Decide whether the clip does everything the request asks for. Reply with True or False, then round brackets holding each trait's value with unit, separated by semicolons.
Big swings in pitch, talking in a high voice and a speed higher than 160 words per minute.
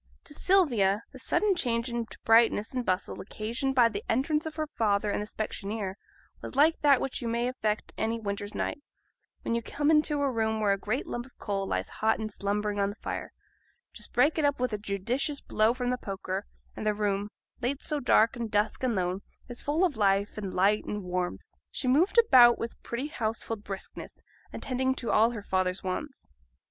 False (4.3 semitones; 230 Hz; 200 wpm)